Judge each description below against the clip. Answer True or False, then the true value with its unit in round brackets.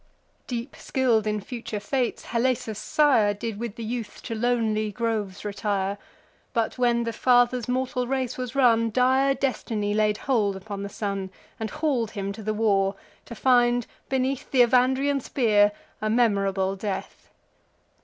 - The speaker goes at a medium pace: True (150 wpm)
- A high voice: True (230 Hz)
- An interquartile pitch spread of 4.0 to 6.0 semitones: False (3.3 semitones)